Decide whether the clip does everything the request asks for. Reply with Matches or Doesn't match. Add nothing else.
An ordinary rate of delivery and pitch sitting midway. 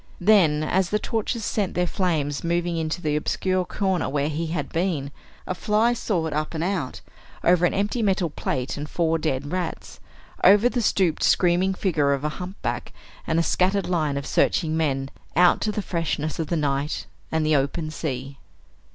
Matches